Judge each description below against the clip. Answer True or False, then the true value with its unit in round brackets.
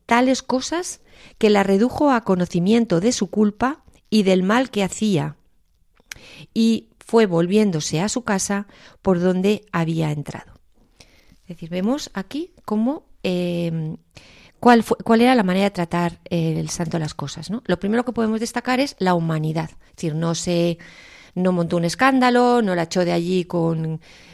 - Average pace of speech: True (165 wpm)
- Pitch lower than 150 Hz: False (190 Hz)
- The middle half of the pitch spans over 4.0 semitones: True (5.3 semitones)